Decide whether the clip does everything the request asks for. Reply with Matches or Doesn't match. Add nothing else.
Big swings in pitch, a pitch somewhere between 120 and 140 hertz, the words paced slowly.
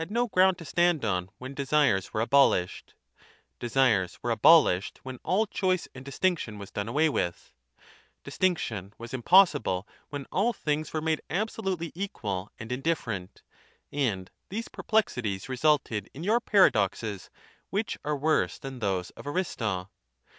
Doesn't match